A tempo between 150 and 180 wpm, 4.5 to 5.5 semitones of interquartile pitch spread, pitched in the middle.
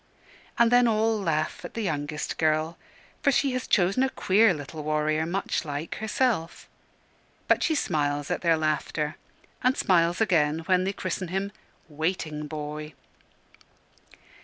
No: average, 140 wpm; average, 4.9 semitones; medium, 165 Hz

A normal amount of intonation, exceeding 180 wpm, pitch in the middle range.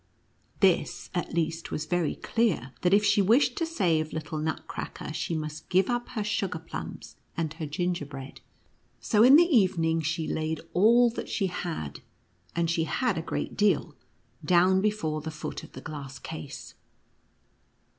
No: average, 4.7 semitones; average, 170 wpm; medium, 170 Hz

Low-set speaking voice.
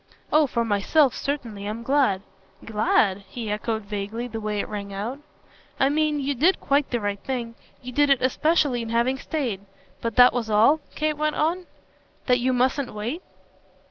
No: high, 245 Hz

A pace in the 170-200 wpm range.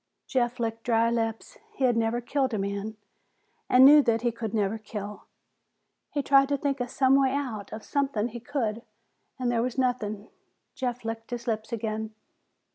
Yes: average, 185 wpm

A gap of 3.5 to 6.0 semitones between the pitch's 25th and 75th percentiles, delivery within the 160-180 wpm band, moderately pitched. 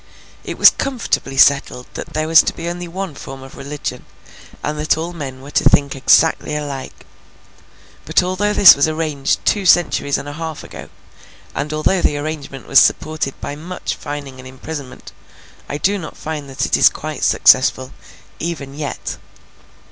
No: average, 3.0 semitones; average, 170 wpm; medium, 150 Hz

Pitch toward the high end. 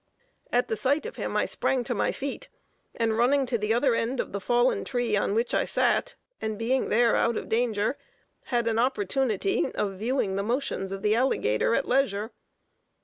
Yes: high, 235 Hz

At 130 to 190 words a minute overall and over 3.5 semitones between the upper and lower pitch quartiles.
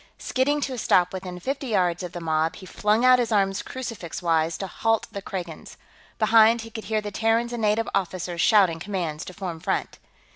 No: fast, 205 wpm; average, 4.3 semitones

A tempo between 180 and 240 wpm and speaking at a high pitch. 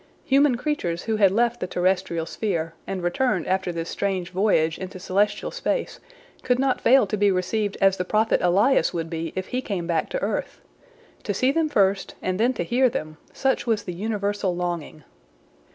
Yes: average, 185 wpm; high, 195 Hz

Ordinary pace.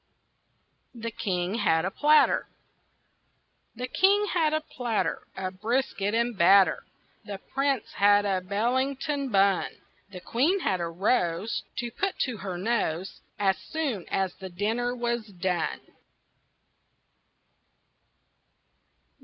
No: slow, 115 wpm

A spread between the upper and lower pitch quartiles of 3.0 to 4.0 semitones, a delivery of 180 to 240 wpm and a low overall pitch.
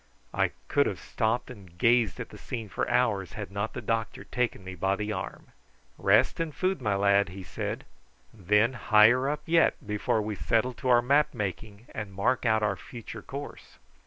Yes: average, 3.6 semitones; average, 190 wpm; low, 110 Hz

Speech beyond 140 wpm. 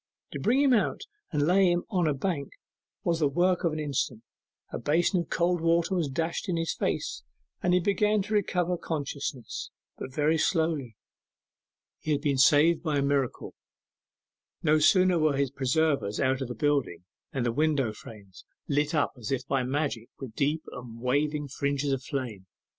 Yes: average, 180 wpm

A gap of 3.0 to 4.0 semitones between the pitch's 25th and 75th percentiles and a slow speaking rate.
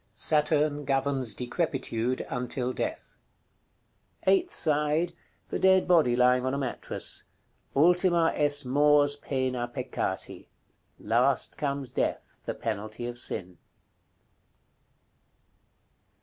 Yes: average, 3.3 semitones; slow, 95 wpm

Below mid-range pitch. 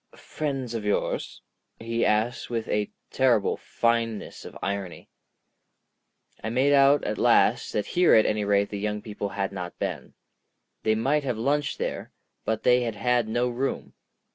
Yes: low, 115 Hz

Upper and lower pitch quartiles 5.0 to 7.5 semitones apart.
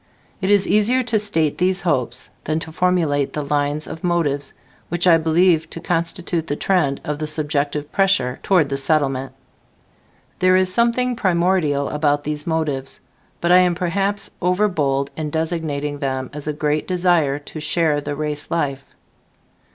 No: average, 3.8 semitones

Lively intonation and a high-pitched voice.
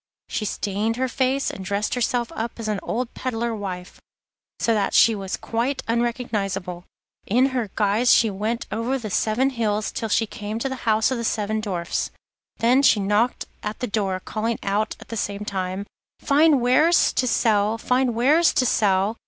No: average, 3.2 semitones; high, 225 Hz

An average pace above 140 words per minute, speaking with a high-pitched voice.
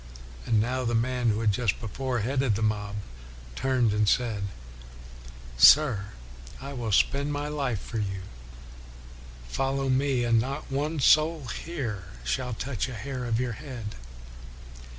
No: average, 150 wpm; low, 120 Hz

